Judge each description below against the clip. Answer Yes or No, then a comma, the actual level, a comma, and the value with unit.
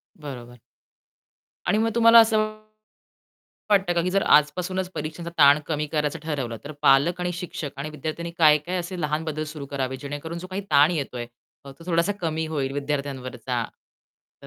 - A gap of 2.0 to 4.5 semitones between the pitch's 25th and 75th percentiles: Yes, average, 3.7 semitones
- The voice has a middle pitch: Yes, medium, 155 Hz